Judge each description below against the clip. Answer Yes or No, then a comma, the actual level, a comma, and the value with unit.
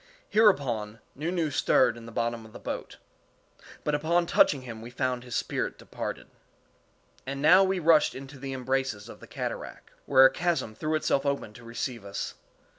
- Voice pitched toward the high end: No, low, 135 Hz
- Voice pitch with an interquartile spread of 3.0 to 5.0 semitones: Yes, average, 4.7 semitones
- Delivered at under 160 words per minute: No, average, 180 wpm